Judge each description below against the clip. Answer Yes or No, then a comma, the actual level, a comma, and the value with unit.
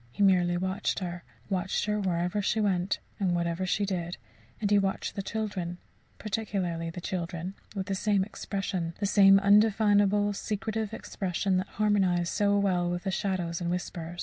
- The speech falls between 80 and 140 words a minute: No, average, 165 wpm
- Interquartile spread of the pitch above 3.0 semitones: No, narrow, 2.6 semitones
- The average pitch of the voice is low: No, high, 190 Hz